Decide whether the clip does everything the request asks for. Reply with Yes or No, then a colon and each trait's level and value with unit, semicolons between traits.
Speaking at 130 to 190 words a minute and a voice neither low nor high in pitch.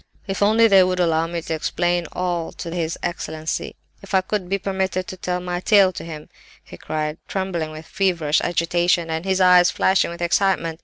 No: average, 200 wpm; medium, 175 Hz